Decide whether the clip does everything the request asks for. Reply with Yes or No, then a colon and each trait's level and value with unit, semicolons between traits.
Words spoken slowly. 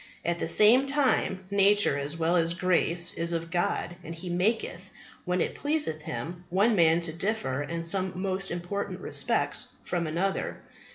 No: average, 165 wpm